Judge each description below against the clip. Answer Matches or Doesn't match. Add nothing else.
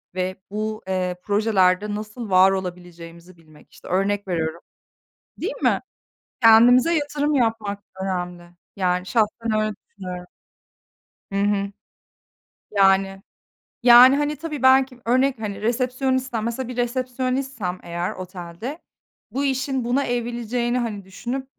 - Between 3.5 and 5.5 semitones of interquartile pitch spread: Matches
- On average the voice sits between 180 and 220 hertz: Matches